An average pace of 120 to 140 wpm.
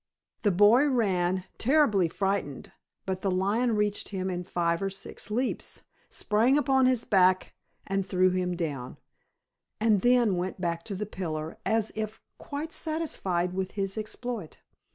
No: average, 150 wpm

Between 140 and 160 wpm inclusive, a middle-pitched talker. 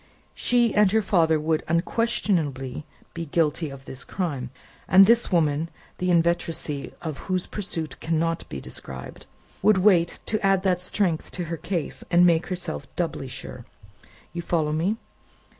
Yes: average, 150 wpm; medium, 170 Hz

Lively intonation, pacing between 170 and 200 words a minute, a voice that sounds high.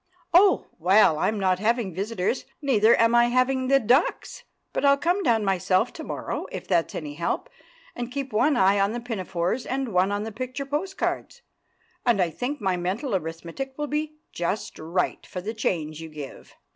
Yes: wide, 6.4 semitones; average, 185 wpm; high, 220 Hz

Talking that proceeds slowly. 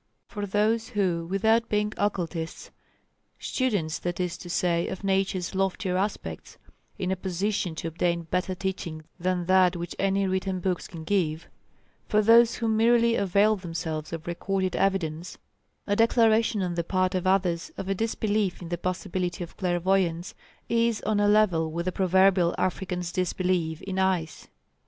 No: average, 155 wpm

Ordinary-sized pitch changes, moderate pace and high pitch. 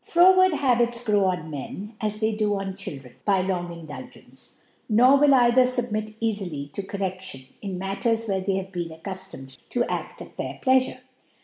Yes: average, 4.8 semitones; average, 170 wpm; high, 200 Hz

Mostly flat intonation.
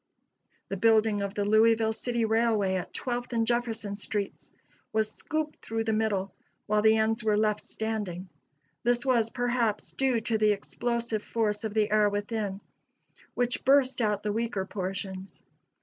Yes: narrow, 2.0 semitones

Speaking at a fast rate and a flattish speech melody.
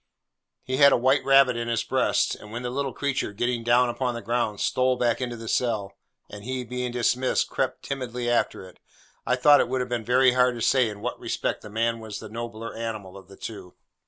Yes: fast, 225 wpm; narrow, 2.0 semitones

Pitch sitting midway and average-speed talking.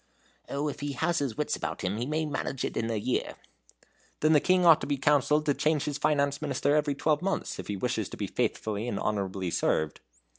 No: medium, 145 Hz; fast, 225 wpm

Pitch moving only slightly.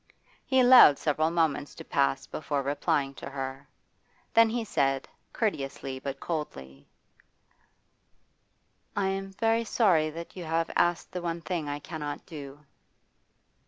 No: average, 4.8 semitones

